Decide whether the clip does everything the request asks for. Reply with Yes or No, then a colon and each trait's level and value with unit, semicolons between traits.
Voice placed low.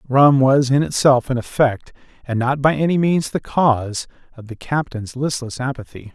Yes: low, 130 Hz